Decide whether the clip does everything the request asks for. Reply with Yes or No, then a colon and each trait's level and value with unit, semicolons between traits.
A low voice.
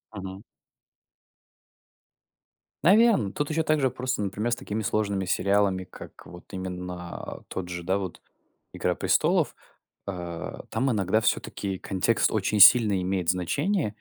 Yes: low, 100 Hz